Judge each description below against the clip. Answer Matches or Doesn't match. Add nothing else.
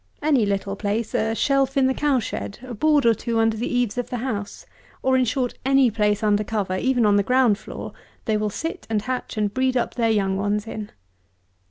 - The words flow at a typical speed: Doesn't match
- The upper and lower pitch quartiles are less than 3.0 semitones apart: Doesn't match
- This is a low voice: Doesn't match